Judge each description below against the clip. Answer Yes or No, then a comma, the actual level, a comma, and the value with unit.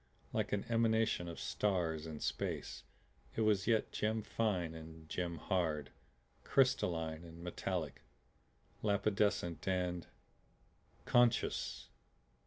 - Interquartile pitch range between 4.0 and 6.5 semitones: Yes, average, 4.6 semitones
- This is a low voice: Yes, very low, 90 Hz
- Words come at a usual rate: No, slow, 100 wpm